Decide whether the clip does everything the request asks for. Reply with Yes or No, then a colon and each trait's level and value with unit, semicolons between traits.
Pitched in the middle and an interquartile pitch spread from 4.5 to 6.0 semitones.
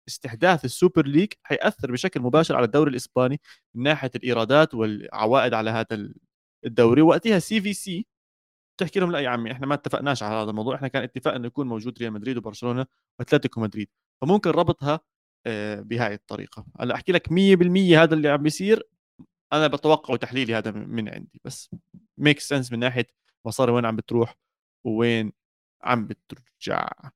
No: low, 130 Hz; wide, 5.5 semitones